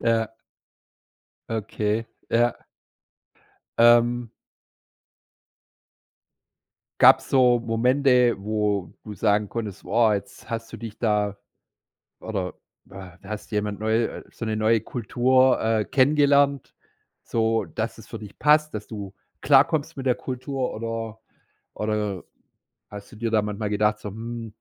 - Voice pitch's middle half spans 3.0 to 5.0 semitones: No, narrow, 2.5 semitones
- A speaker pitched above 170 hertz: No, low, 115 Hz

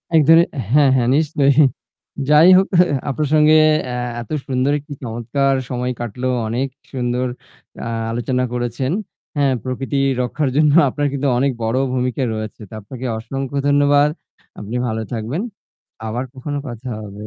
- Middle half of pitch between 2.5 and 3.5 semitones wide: Yes, average, 3.0 semitones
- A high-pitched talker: No, low, 130 Hz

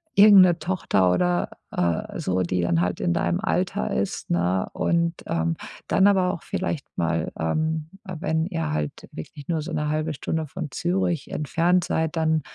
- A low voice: No, medium, 155 Hz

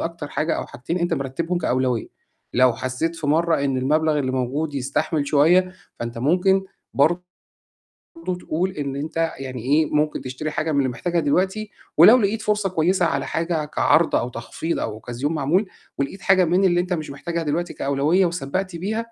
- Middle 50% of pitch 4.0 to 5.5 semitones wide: Yes, average, 4.3 semitones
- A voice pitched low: No, medium, 160 Hz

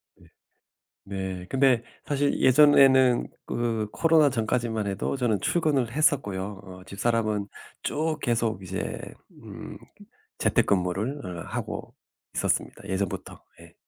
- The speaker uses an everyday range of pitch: No, wide, 5.7 semitones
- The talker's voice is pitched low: Yes, low, 115 Hz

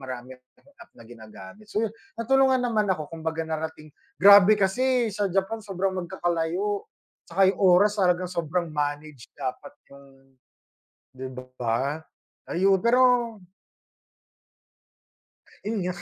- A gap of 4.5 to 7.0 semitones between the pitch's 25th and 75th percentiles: Yes, average, 5.1 semitones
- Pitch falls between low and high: Yes, medium, 180 Hz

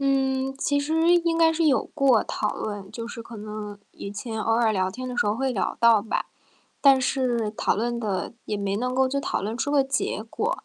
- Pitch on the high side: Yes, high, 240 Hz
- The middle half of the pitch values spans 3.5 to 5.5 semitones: Yes, average, 4.3 semitones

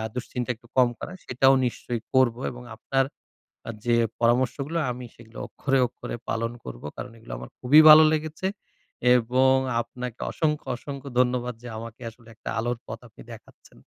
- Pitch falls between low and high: No, low, 125 Hz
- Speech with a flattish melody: Yes, narrow, 2.3 semitones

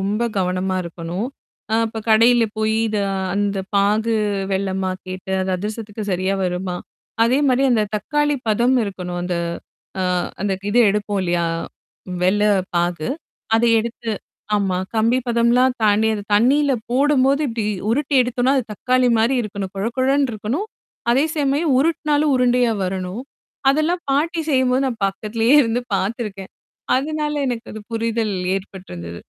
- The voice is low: No, high, 225 Hz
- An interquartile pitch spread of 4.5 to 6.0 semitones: Yes, average, 4.8 semitones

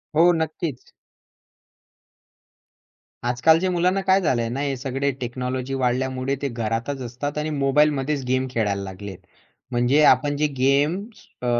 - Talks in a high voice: No, low, 135 Hz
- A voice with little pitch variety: No, average, 3.3 semitones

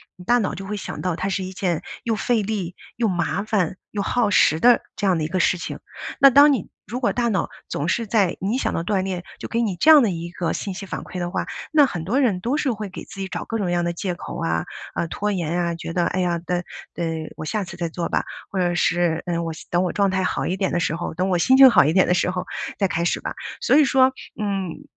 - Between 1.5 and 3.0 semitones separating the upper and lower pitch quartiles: No, average, 3.8 semitones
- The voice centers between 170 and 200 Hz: Yes, medium, 185 Hz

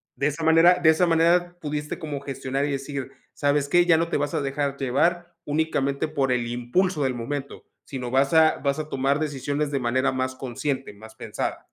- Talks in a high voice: No, medium, 145 Hz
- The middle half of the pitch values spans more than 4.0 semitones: No, average, 3.0 semitones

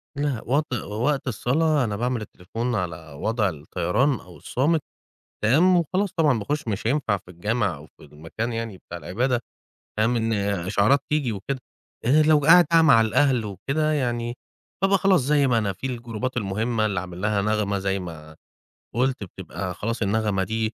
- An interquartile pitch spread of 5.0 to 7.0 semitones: Yes, wide, 5.5 semitones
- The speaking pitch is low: Yes, low, 115 Hz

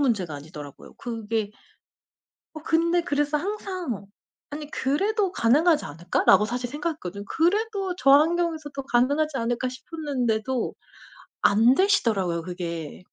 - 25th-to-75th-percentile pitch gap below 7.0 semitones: No, wide, 7.4 semitones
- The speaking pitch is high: Yes, very high, 265 Hz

